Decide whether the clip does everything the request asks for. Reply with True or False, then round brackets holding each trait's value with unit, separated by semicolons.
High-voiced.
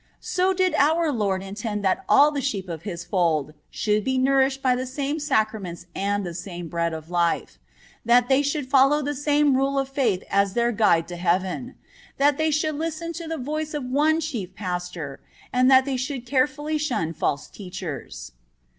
True (250 Hz)